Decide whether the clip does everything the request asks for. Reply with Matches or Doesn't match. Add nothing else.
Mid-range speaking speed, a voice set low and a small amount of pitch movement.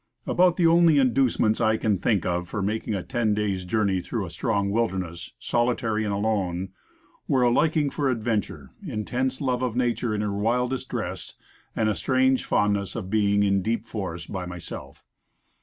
Doesn't match